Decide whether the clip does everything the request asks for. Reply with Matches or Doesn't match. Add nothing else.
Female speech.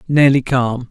Doesn't match